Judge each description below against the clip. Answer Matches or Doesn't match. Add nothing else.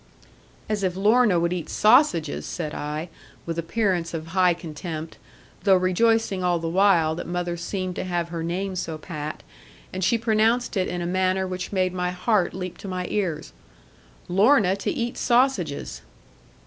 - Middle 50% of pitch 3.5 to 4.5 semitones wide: Doesn't match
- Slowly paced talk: Doesn't match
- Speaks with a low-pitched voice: Doesn't match